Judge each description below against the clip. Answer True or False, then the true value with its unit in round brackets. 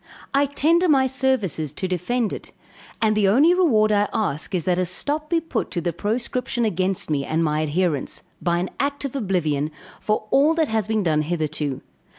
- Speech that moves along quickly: False (190 wpm)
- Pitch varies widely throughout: True (7.8 semitones)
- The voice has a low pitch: False (205 Hz)